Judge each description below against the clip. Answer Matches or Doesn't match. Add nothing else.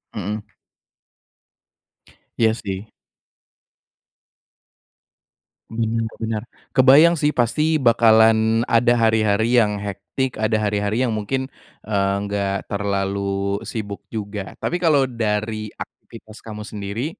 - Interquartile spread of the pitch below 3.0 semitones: Matches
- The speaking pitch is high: Doesn't match